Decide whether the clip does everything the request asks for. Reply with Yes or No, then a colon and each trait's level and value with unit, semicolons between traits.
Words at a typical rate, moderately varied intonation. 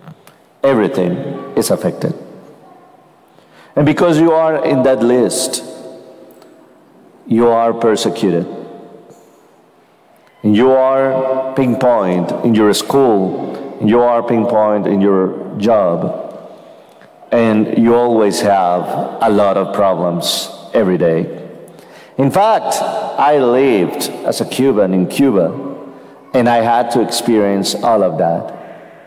No: slow, 105 wpm; average, 3.8 semitones